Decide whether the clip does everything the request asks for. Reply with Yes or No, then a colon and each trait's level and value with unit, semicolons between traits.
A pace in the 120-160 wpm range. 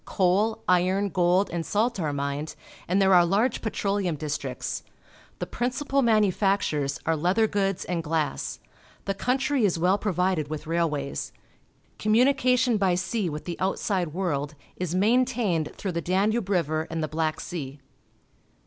Yes: average, 150 wpm